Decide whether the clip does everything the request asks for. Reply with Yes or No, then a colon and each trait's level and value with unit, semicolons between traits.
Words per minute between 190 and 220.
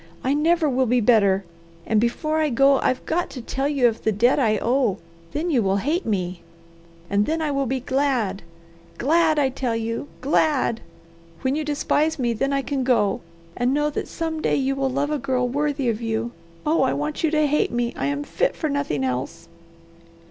Yes: fast, 205 wpm